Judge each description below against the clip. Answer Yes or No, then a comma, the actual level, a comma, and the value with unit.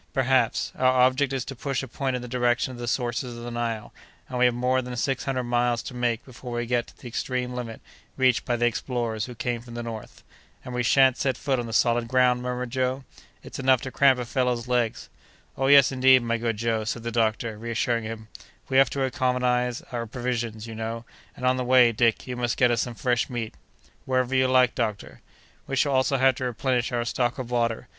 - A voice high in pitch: No, low, 125 Hz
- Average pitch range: No, narrow, 1.5 semitones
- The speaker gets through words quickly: Yes, fast, 225 wpm